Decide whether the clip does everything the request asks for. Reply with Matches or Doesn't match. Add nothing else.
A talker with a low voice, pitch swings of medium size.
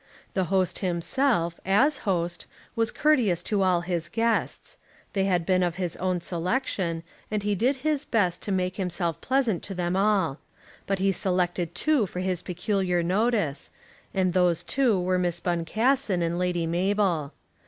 Doesn't match